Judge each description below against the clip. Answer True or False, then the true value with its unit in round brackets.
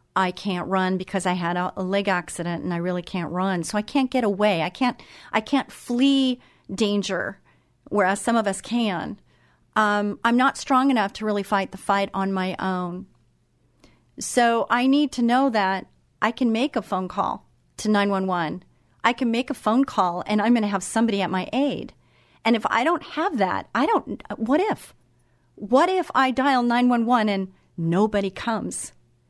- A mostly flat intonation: False (4.6 semitones)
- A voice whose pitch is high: True (210 Hz)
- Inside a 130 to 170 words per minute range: False (185 wpm)